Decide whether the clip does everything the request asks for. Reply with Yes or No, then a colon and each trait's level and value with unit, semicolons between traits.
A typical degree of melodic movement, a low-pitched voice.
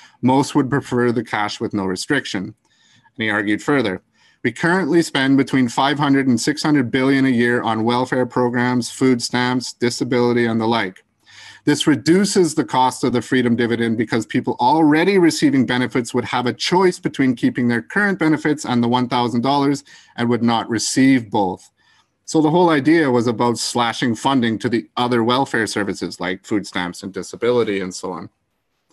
Yes: average, 3.1 semitones; low, 125 Hz